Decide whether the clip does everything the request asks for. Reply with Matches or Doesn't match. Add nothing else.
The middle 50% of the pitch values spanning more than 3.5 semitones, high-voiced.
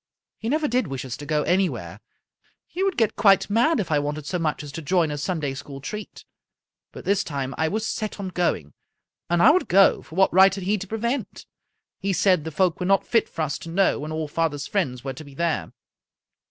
Doesn't match